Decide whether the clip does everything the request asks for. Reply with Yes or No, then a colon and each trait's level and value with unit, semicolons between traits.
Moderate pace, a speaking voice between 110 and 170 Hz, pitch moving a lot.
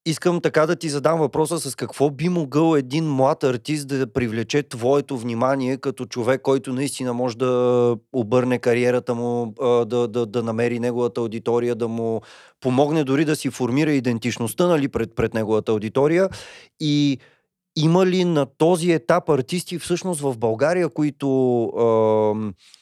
No: average, 145 wpm; low, 130 Hz; average, 4.2 semitones